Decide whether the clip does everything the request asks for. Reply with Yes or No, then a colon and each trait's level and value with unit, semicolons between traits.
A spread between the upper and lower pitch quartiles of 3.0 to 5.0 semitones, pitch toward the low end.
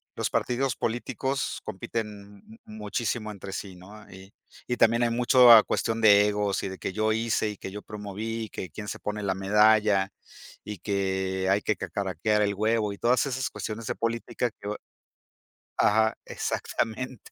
No: narrow, 2.4 semitones; low, 105 Hz